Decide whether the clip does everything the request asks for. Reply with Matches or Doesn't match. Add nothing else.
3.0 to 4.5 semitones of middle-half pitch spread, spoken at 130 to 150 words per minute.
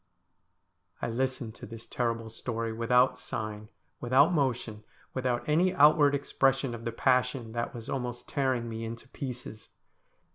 Doesn't match